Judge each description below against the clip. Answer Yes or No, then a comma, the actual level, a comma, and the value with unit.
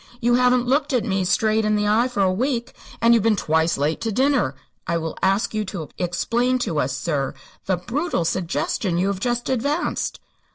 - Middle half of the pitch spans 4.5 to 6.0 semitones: Yes, wide, 5.6 semitones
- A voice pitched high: Yes, high, 215 Hz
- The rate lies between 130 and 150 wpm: No, average, 195 wpm